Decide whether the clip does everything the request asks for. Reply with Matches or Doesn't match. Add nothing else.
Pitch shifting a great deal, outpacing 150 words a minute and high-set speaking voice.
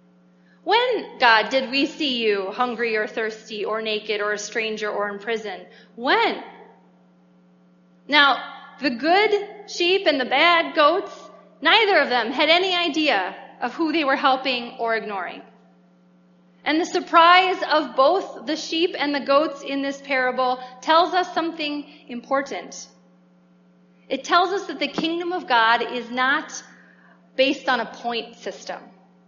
Doesn't match